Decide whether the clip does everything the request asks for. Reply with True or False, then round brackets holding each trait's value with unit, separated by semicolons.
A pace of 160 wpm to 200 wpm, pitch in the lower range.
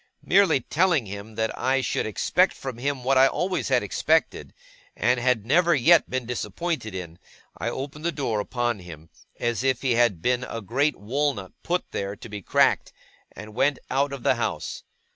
True (180 wpm; 125 Hz)